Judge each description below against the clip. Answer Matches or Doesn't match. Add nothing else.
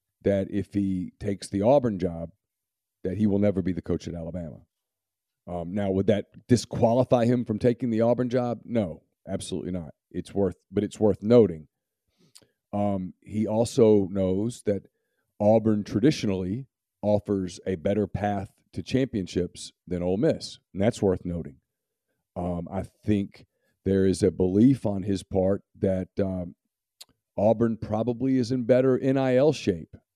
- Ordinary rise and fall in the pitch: Matches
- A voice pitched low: Matches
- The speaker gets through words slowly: Doesn't match